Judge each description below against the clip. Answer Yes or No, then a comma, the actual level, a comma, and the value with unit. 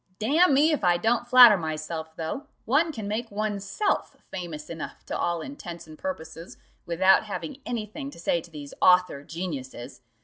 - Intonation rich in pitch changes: Yes, wide, 7.0 semitones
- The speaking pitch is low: No, high, 190 Hz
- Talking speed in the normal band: Yes, average, 170 wpm